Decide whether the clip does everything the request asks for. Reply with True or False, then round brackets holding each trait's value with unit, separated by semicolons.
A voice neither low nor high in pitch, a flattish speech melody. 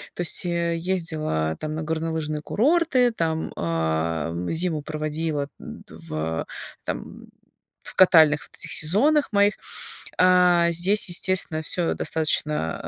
False (160 Hz; 3.3 semitones)